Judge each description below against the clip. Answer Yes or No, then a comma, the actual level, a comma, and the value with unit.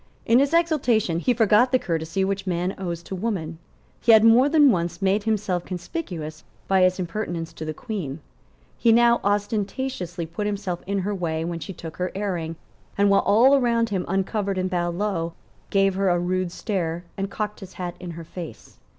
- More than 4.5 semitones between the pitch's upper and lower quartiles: No, average, 3.7 semitones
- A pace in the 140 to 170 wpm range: No, average, 190 wpm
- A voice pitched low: No, high, 190 Hz